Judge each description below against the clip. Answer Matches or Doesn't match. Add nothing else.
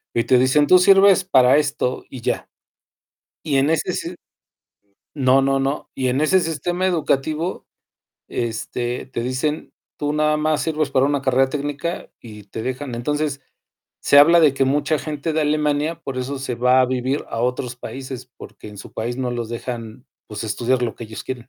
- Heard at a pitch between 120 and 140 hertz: Matches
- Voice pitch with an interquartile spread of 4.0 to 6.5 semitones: Doesn't match